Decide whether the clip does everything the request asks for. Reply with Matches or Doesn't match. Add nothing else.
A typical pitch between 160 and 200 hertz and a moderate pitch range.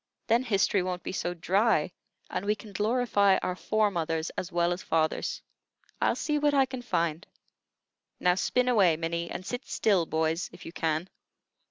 Matches